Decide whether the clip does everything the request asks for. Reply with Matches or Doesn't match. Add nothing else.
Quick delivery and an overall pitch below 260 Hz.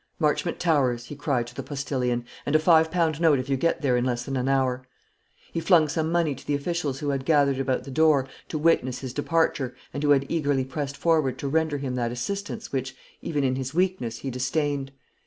Matches